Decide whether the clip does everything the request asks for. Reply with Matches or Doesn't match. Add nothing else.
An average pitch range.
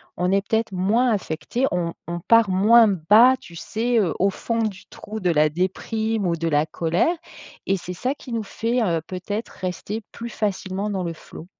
Matches